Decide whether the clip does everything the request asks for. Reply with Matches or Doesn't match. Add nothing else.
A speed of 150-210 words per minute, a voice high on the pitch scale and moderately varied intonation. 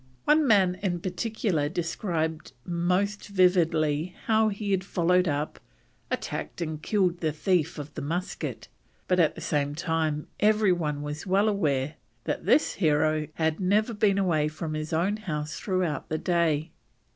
Doesn't match